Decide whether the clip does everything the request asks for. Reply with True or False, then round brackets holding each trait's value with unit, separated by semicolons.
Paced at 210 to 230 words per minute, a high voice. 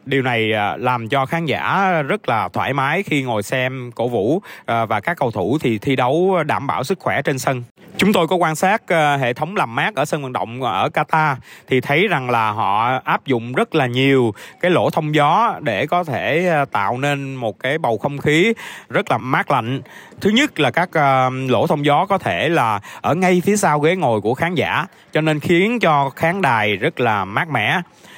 False (215 wpm; 145 Hz)